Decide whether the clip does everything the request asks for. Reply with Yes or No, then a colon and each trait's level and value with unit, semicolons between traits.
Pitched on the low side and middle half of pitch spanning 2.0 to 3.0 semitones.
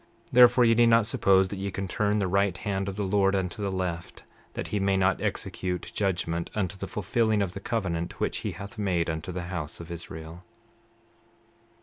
Yes: very low, 95 Hz; narrow, 2.5 semitones